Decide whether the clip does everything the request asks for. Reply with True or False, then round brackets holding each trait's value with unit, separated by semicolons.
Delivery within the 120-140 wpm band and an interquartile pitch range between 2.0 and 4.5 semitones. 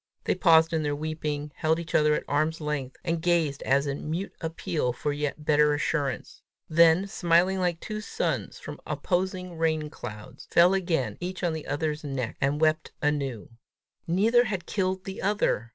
False (170 wpm; 3.2 semitones)